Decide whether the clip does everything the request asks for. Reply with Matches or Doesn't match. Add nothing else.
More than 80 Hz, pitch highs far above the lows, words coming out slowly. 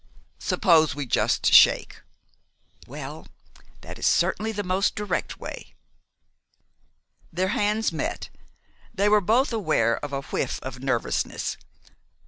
Matches